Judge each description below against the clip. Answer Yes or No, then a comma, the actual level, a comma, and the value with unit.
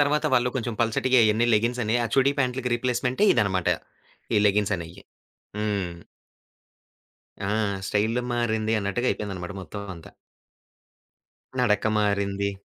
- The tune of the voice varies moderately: Yes, average, 3.6 semitones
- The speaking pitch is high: No, low, 110 Hz